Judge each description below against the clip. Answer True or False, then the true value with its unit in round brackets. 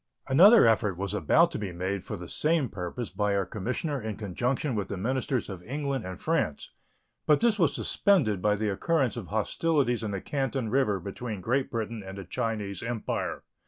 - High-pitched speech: False (110 Hz)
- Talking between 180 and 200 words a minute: True (190 wpm)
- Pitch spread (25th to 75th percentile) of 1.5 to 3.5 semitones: False (5.3 semitones)